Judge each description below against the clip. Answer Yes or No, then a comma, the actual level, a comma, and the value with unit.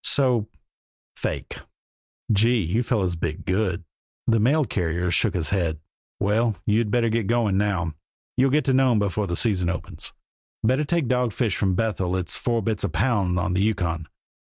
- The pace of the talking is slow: No, average, 165 wpm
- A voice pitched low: Yes, low, 105 Hz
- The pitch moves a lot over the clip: No, average, 4.6 semitones